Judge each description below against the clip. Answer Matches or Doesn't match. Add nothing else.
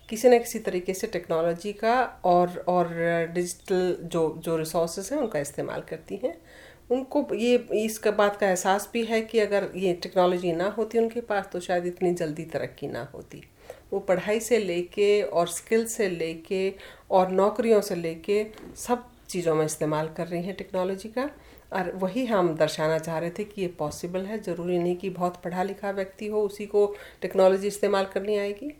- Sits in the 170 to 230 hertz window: Matches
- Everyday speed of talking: Matches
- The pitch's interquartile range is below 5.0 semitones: Matches